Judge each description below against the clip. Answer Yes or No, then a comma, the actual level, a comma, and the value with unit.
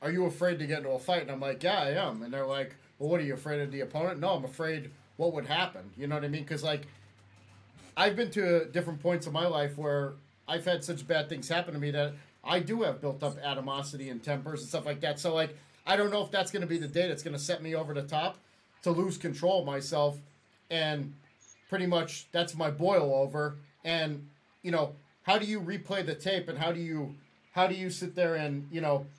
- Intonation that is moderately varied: Yes, average, 3.6 semitones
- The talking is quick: Yes, fast, 250 wpm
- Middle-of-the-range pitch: Yes, medium, 155 Hz